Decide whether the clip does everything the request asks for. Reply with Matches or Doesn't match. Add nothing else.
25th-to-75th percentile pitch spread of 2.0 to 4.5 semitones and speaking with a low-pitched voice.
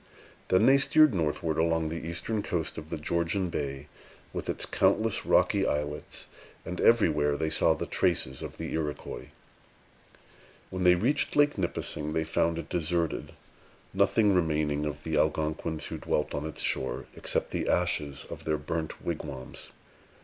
Matches